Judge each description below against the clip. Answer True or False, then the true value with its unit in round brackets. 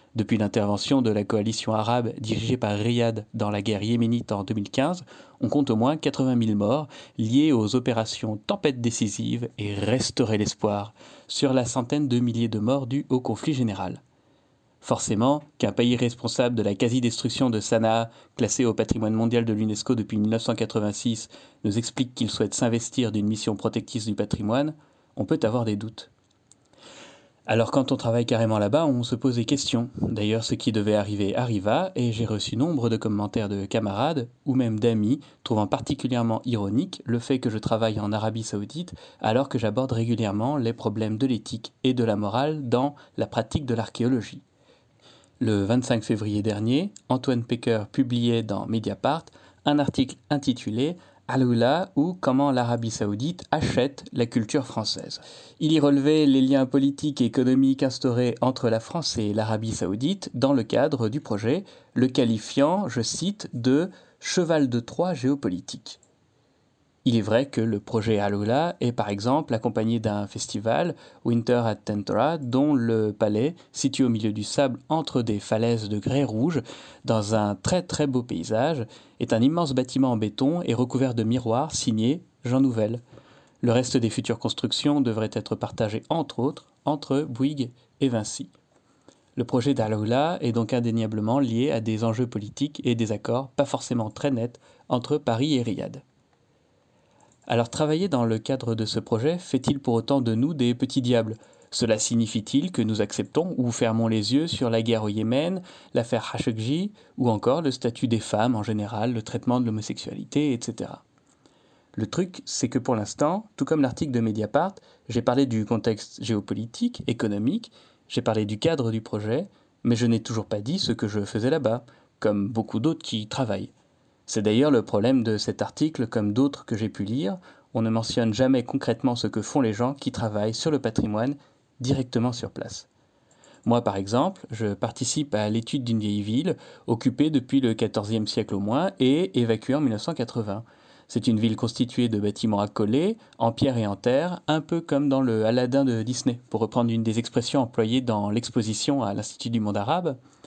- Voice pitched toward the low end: True (120 Hz)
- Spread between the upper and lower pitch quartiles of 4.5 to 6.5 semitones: False (3.4 semitones)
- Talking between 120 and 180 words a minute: True (175 wpm)